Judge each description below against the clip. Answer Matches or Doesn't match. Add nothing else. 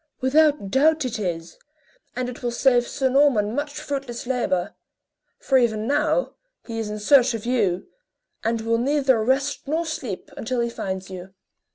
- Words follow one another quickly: Doesn't match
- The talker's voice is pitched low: Doesn't match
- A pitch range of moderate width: Matches